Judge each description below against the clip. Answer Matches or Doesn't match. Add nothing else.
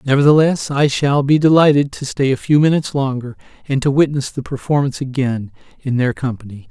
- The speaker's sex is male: Matches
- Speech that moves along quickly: Doesn't match